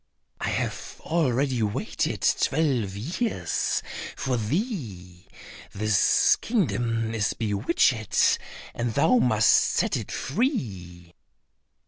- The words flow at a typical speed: No, slow, 90 wpm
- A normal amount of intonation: No, wide, 6.4 semitones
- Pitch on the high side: No, low, 115 Hz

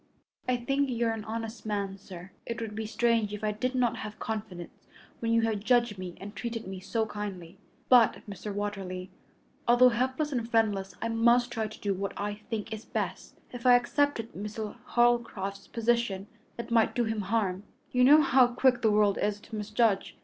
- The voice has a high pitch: Yes, high, 220 Hz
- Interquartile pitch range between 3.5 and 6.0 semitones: No, average, 2.7 semitones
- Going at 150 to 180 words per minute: No, average, 195 wpm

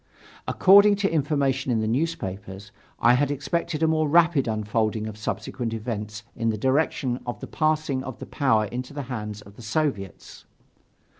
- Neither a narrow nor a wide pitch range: No, wide, 6.0 semitones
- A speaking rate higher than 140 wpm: Yes, average, 165 wpm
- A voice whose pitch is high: No, low, 125 Hz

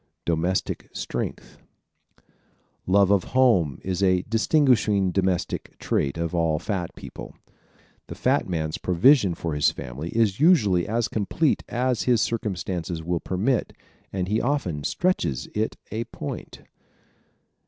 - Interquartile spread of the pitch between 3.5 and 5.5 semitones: Yes, average, 5.1 semitones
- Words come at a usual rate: No, slow, 130 wpm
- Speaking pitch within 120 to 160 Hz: No, very low, 95 Hz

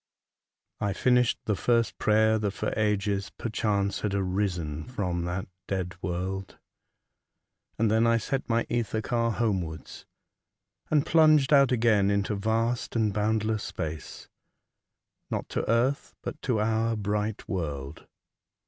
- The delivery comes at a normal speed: No, slow, 130 wpm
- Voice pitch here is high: No, low, 105 Hz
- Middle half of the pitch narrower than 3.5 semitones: Yes, average, 3.1 semitones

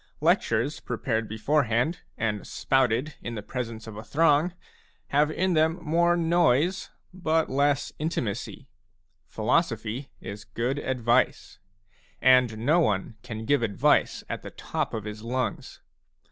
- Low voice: Yes, low, 130 Hz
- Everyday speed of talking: No, slow, 130 wpm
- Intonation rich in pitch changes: Yes, wide, 5.7 semitones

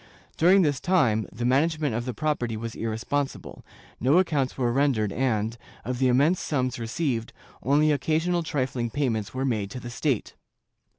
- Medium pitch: No, low, 130 Hz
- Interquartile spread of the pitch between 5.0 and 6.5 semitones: No, average, 4.4 semitones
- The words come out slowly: No, average, 160 wpm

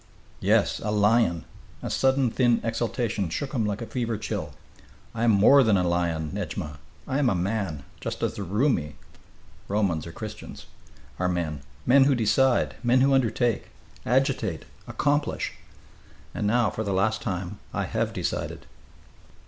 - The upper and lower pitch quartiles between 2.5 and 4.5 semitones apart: No, average, 5.2 semitones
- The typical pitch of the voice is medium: No, low, 110 Hz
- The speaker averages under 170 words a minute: Yes, average, 155 wpm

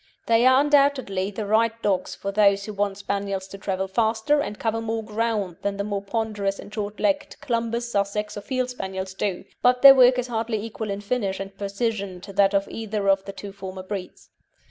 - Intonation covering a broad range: No, narrow, 2.6 semitones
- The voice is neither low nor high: No, high, 205 Hz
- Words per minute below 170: No, fast, 205 wpm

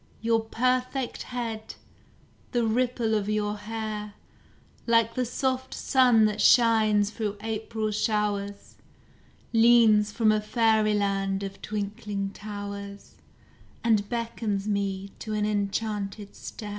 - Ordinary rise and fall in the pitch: No, narrow, 2.0 semitones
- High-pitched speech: Yes, high, 215 Hz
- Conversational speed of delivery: No, slow, 110 wpm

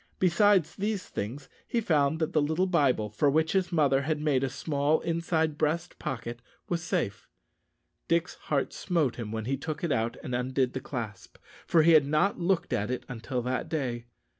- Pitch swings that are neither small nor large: Yes, average, 4.8 semitones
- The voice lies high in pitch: No, medium, 150 Hz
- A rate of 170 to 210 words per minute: Yes, average, 190 wpm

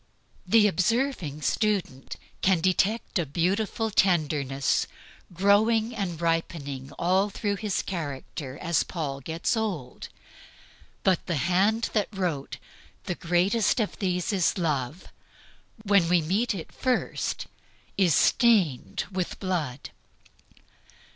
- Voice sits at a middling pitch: Yes, medium, 180 Hz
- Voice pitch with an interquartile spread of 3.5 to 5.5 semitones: Yes, average, 4.6 semitones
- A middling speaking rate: No, slow, 110 wpm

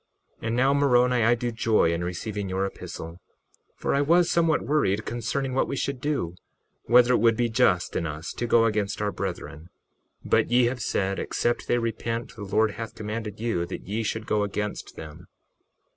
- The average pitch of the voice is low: Yes, low, 115 Hz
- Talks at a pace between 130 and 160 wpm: No, average, 195 wpm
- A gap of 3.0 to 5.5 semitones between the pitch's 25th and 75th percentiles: Yes, average, 3.7 semitones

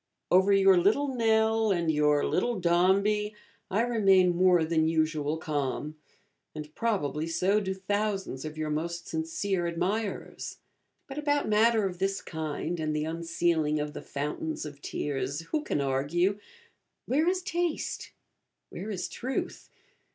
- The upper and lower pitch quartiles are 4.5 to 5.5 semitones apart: Yes, average, 5.2 semitones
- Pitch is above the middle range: No, medium, 175 Hz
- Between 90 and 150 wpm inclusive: Yes, average, 140 wpm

